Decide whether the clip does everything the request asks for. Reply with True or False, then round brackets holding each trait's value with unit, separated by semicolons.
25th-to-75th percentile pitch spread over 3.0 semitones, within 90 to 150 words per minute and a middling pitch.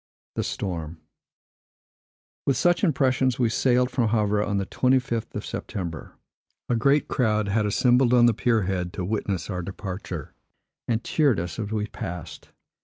False (4.1 semitones; 145 wpm; 110 Hz)